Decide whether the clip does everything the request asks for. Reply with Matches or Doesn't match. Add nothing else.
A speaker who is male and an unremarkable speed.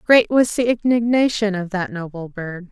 Doesn't match